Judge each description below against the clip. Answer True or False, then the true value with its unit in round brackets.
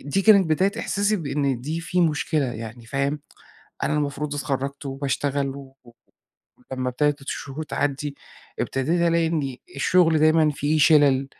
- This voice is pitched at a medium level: True (145 Hz)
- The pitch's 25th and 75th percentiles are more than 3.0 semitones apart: False (2.6 semitones)